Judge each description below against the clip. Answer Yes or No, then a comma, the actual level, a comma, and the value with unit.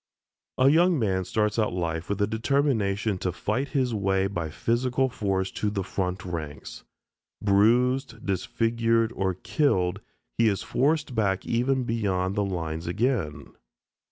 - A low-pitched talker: Yes, low, 105 Hz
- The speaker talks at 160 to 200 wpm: No, average, 145 wpm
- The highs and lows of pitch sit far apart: No, average, 4.4 semitones